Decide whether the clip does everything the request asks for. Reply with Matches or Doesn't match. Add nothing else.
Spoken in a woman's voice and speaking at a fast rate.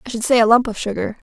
Matches